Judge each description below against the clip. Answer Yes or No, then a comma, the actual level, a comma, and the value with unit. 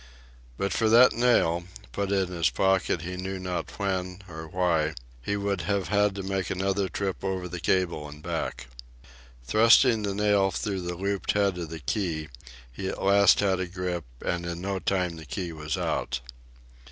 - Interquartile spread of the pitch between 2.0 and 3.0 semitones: Yes, narrow, 2.4 semitones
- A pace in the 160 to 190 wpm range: Yes, average, 180 wpm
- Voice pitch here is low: Yes, very low, 95 Hz